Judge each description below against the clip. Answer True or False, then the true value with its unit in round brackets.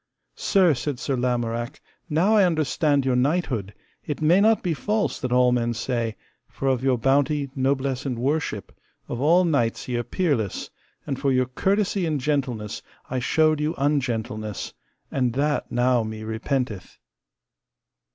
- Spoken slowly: False (150 wpm)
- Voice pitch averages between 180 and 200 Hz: False (135 Hz)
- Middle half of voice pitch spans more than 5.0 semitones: False (4.0 semitones)